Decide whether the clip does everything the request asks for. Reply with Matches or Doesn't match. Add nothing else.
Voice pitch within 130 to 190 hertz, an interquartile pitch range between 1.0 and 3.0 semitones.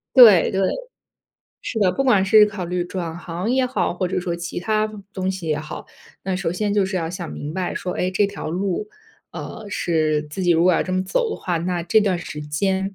Matches